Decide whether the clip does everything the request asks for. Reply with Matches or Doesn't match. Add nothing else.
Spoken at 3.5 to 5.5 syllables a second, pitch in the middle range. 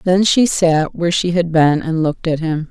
Matches